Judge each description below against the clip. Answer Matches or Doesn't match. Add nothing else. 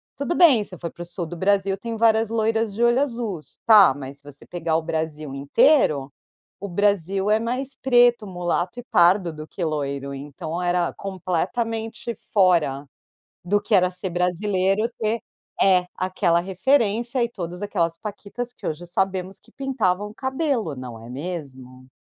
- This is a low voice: Doesn't match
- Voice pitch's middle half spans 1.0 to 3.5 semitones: Doesn't match